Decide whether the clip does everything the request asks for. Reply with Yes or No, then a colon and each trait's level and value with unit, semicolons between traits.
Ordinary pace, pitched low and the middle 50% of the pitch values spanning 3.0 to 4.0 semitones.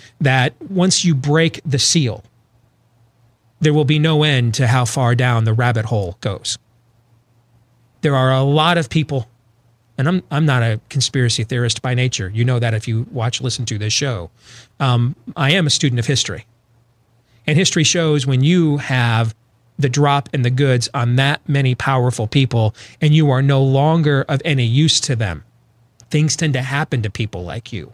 Yes: average, 185 wpm; low, 125 Hz; average, 3.4 semitones